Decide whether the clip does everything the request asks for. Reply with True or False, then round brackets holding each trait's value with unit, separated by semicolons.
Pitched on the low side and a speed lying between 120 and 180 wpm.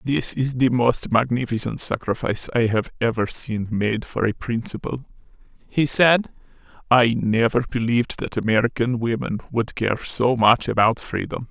True (120 Hz; 145 wpm)